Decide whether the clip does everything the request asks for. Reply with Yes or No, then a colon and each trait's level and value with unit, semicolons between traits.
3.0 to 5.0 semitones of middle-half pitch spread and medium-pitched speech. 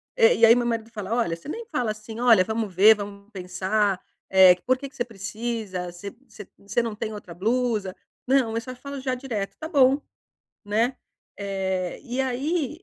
No: average, 4.1 semitones; high, 225 Hz